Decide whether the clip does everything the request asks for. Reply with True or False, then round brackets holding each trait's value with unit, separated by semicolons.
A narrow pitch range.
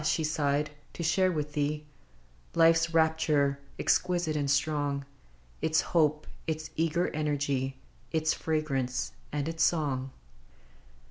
True (2.1 semitones)